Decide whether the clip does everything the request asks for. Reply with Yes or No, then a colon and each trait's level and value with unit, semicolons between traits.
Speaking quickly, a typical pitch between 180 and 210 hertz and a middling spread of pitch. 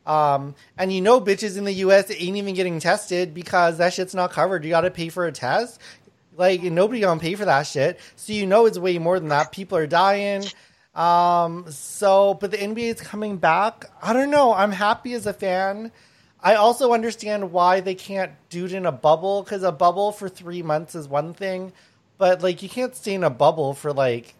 Yes: fast, 215 wpm; medium, 185 Hz; average, 3.0 semitones